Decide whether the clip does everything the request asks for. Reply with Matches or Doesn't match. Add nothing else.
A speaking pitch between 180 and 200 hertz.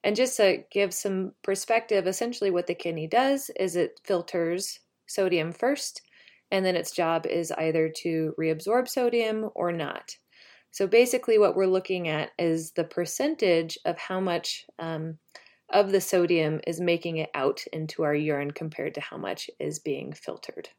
Matches